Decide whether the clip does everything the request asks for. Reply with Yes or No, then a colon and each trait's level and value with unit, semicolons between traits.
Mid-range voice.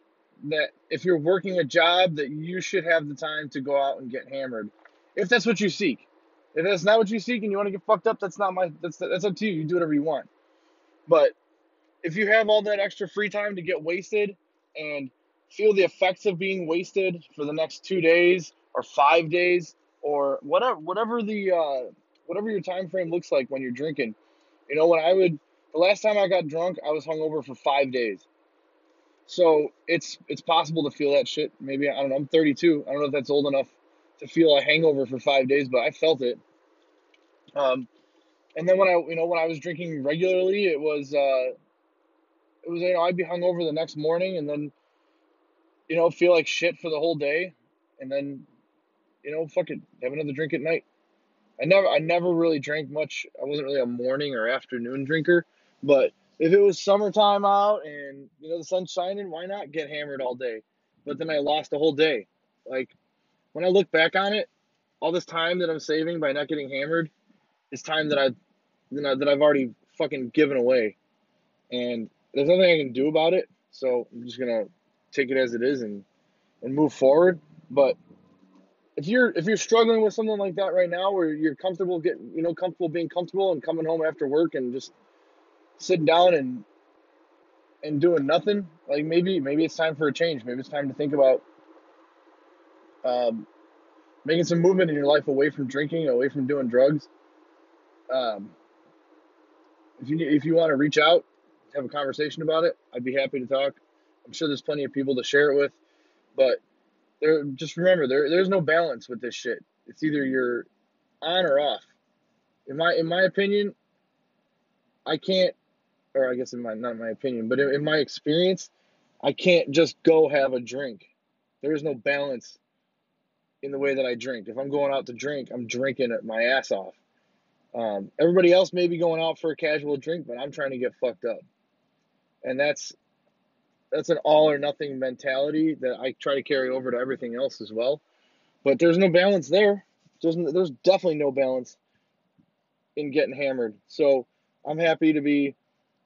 Yes: medium, 160 Hz